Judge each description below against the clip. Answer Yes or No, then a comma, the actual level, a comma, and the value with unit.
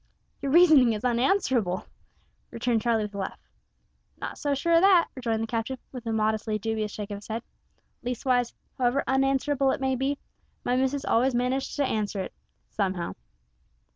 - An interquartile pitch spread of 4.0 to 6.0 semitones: No, average, 3.6 semitones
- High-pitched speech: Yes, high, 245 Hz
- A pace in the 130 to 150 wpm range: No, average, 170 wpm